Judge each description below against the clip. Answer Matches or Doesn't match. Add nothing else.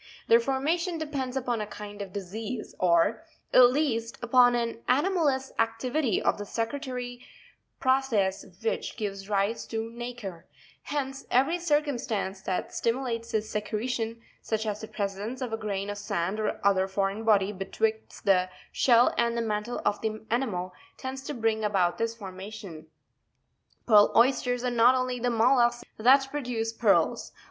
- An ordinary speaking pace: Matches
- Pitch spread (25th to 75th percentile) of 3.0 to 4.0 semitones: Matches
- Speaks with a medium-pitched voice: Doesn't match